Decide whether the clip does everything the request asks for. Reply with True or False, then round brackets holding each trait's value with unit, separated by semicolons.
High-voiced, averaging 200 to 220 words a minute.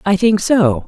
True (200 Hz; 205 wpm)